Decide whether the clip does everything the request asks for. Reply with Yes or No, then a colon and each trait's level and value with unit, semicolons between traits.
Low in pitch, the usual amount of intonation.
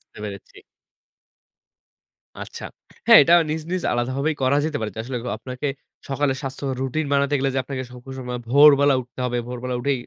No: low, 130 Hz; narrow, 2.3 semitones